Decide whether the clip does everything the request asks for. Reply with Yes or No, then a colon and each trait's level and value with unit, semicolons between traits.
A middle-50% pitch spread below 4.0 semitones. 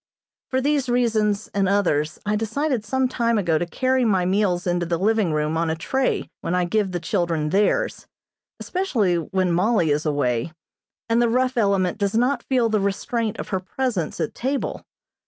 No: wide, 5.5 semitones